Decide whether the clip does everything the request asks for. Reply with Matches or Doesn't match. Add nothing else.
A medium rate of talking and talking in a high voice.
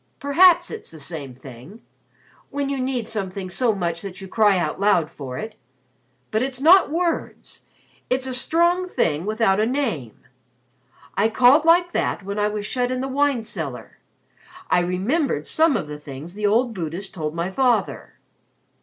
Matches